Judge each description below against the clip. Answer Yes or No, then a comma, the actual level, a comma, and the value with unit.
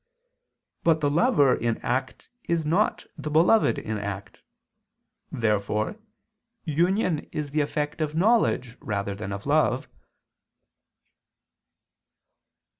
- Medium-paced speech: No, slow, 105 wpm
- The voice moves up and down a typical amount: No, wide, 7.4 semitones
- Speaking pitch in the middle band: Yes, medium, 145 Hz